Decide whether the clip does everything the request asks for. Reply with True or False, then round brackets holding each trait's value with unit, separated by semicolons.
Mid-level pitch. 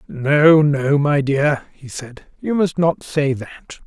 True (145 Hz)